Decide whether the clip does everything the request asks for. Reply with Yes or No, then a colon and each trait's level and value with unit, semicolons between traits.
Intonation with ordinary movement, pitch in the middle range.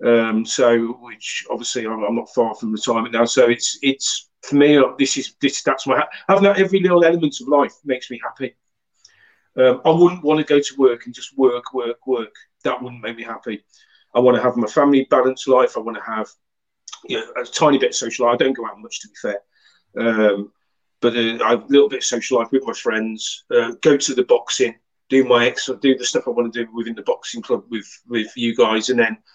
No: average, 3.5 semitones; low, 125 Hz